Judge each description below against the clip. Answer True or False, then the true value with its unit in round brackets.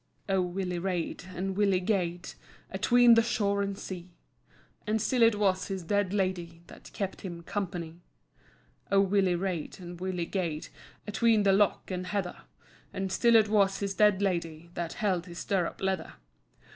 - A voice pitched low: False (190 Hz)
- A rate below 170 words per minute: True (160 wpm)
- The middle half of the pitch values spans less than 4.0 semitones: True (2.4 semitones)